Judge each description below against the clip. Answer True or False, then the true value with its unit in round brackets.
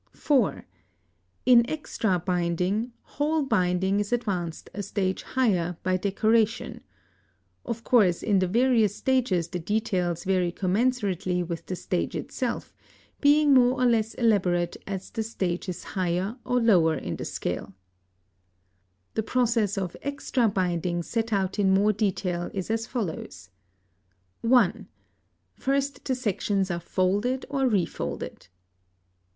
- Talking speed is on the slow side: True (130 wpm)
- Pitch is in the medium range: False (200 Hz)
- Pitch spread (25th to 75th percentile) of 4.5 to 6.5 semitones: True (4.8 semitones)